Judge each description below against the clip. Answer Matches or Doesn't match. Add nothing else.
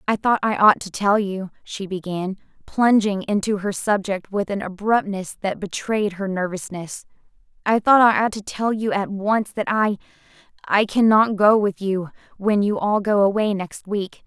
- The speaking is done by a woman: Matches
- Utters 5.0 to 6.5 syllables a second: Doesn't match